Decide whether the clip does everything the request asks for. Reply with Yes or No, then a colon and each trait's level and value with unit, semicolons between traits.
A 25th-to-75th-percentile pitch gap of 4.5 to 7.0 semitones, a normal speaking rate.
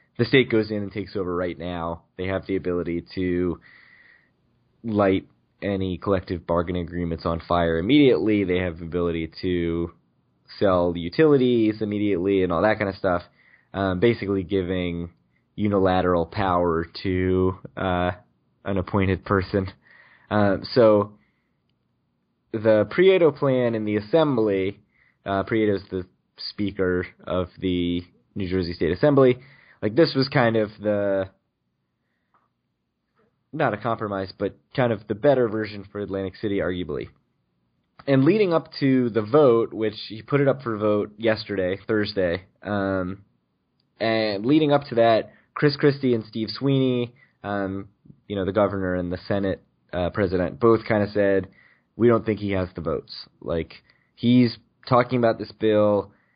No: average, 3.7 semitones; average, 145 wpm